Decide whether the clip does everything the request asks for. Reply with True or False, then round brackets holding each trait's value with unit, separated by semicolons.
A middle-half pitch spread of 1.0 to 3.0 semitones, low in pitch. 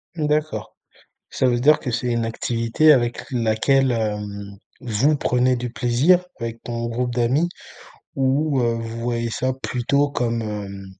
True (2.6 semitones; 120 Hz)